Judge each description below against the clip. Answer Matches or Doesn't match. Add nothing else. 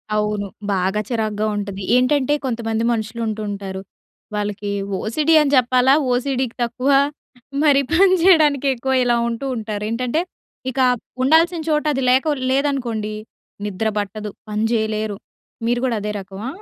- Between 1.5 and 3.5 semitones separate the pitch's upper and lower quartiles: Doesn't match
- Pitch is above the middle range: Matches